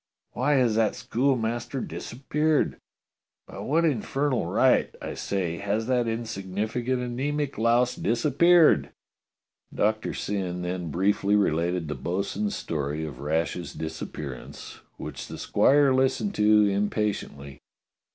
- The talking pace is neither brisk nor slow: No, slow, 120 wpm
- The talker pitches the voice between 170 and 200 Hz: No, low, 110 Hz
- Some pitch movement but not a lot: No, wide, 6.4 semitones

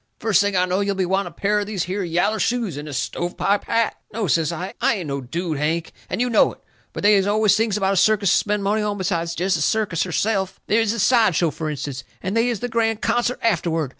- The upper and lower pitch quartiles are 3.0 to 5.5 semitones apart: Yes, average, 4.2 semitones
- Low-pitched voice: No, high, 195 Hz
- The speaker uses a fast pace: Yes, fast, 265 wpm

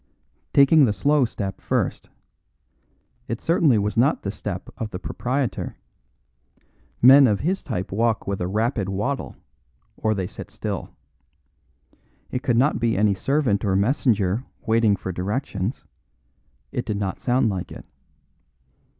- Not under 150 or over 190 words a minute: No, average, 140 wpm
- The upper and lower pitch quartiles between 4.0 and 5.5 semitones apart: Yes, average, 4.7 semitones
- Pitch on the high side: No, low, 110 Hz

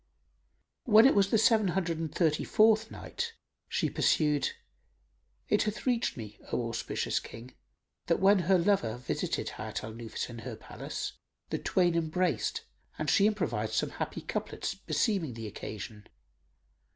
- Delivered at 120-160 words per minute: Yes, average, 150 wpm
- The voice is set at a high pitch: No, medium, 170 Hz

